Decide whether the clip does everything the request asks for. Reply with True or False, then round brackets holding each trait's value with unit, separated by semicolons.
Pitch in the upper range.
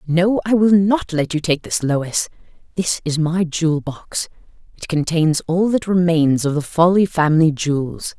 False (165 Hz)